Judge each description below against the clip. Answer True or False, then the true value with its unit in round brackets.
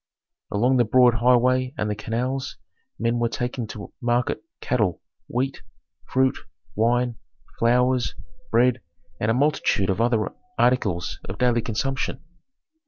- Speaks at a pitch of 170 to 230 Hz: False (120 Hz)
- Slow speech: True (125 wpm)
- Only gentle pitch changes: True (2.2 semitones)